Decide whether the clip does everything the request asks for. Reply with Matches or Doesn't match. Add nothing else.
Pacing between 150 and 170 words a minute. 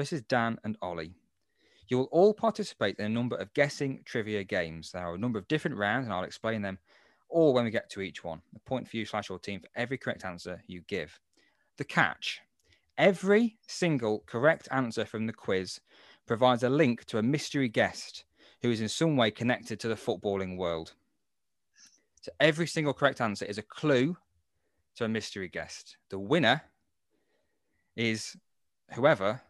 Doesn't match